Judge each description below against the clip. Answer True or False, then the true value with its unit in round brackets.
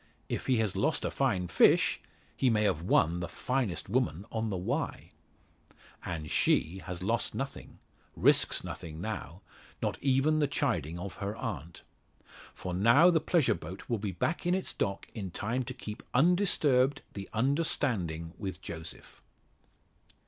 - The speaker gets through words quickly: False (155 wpm)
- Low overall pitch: True (105 Hz)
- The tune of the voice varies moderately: False (6.9 semitones)